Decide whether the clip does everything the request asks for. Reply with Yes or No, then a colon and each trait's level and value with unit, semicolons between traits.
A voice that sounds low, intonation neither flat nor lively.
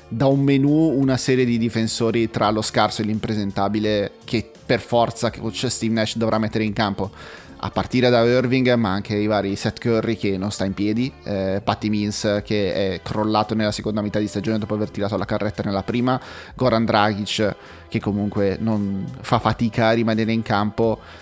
No: low, 110 Hz; narrow, 2.0 semitones